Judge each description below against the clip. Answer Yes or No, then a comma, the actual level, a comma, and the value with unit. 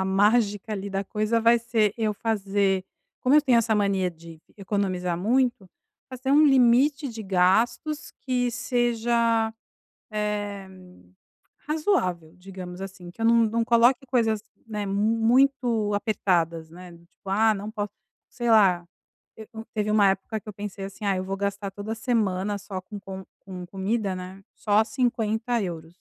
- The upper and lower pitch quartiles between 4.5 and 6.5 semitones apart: No, average, 3.3 semitones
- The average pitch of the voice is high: Yes, high, 210 Hz